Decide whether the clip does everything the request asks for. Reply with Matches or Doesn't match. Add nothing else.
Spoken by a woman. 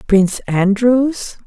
Matches